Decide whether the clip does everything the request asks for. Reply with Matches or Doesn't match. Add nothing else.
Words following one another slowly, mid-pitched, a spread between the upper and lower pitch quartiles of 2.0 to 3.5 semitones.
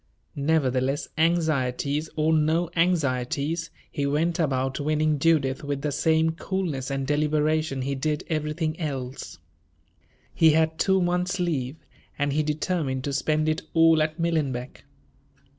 Matches